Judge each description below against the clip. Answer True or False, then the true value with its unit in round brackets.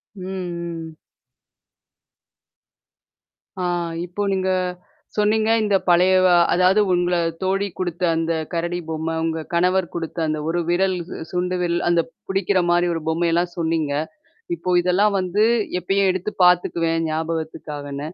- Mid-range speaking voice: True (175 Hz)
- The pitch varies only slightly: True (2.1 semitones)